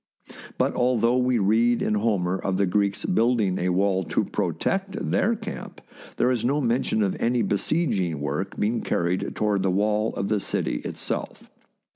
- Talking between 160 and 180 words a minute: Yes, average, 165 wpm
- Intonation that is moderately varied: Yes, average, 4.1 semitones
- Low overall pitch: Yes, low, 105 Hz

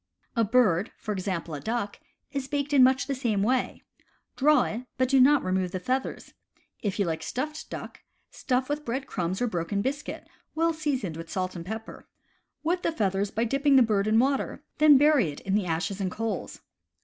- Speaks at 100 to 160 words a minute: No, average, 195 wpm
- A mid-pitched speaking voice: No, high, 230 Hz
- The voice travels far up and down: Yes, wide, 6.1 semitones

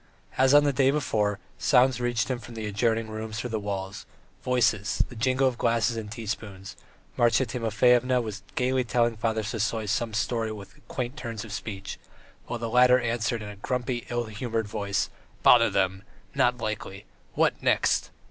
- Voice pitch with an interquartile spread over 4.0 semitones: No, narrow, 2.5 semitones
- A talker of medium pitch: No, low, 115 Hz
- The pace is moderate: Yes, average, 170 wpm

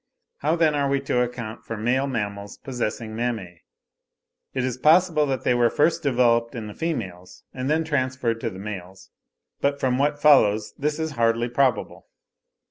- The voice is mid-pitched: No, low, 125 Hz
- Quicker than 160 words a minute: Yes, average, 170 wpm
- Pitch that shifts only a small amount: No, average, 3.9 semitones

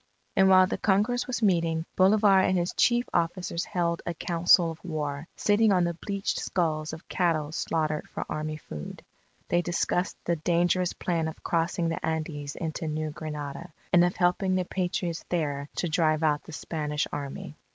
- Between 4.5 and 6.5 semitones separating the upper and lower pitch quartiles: No, average, 2.8 semitones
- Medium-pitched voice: Yes, medium, 170 Hz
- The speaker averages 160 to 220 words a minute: Yes, average, 170 wpm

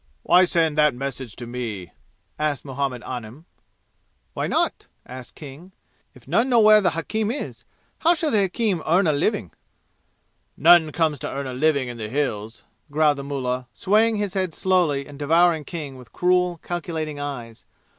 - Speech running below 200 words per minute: Yes, average, 165 wpm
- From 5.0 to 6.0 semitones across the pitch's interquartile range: Yes, wide, 5.4 semitones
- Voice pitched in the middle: Yes, medium, 150 Hz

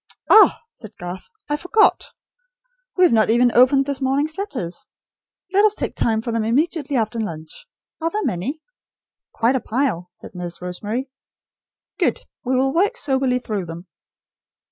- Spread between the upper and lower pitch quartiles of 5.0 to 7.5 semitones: Yes, wide, 5.6 semitones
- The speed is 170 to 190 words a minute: No, average, 155 wpm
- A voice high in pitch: Yes, very high, 250 Hz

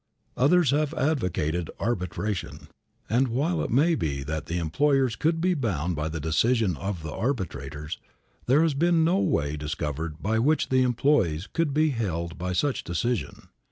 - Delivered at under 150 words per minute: No, average, 160 wpm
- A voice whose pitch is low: Yes, low, 110 Hz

